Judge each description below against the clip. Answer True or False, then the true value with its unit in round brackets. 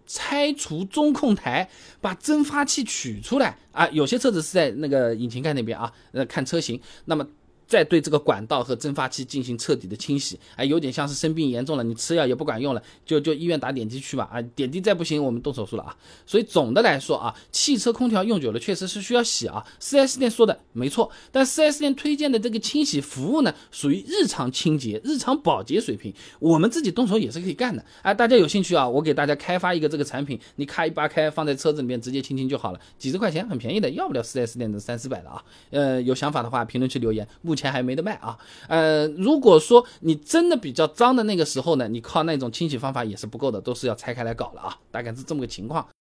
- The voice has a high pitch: False (150 Hz)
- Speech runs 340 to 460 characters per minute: True (360 characters per minute)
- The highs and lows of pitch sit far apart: True (7.7 semitones)